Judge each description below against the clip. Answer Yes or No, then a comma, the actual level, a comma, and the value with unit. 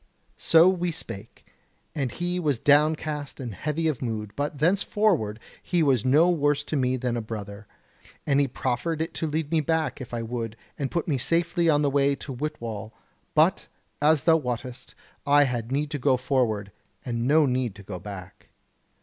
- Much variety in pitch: No, average, 4.7 semitones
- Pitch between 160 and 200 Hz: No, medium, 140 Hz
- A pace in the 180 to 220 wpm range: Yes, average, 185 wpm